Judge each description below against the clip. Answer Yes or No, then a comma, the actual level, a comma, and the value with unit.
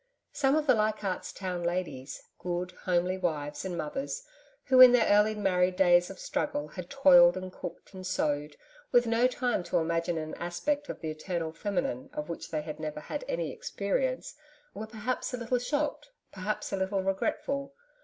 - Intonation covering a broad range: Yes, wide, 6.6 semitones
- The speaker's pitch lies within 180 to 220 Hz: Yes, high, 190 Hz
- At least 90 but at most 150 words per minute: No, average, 175 wpm